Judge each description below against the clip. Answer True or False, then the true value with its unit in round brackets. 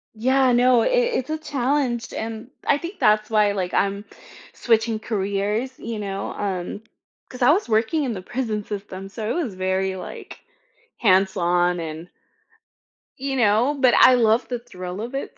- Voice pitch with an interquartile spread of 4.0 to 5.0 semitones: True (4.5 semitones)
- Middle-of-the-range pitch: False (220 Hz)